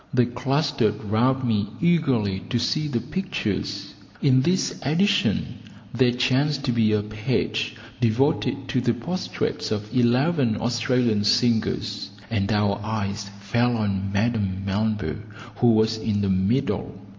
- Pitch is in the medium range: No, low, 115 Hz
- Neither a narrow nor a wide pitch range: Yes, average, 3.9 semitones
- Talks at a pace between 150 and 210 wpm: No, slow, 135 wpm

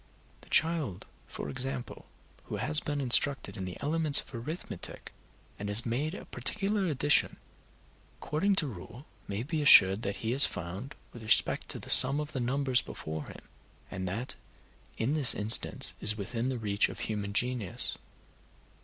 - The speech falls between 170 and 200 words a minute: No, average, 160 wpm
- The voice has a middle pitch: No, low, 125 Hz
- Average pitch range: No, wide, 6.0 semitones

